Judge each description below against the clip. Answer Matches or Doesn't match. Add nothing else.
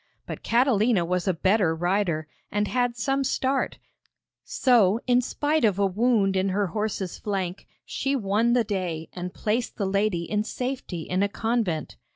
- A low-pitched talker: Doesn't match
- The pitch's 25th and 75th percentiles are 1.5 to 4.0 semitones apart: Doesn't match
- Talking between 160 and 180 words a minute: Matches